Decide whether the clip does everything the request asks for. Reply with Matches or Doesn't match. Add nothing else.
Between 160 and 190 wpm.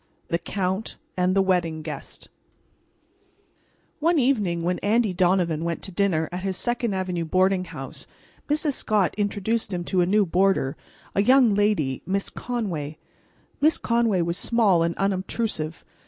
Doesn't match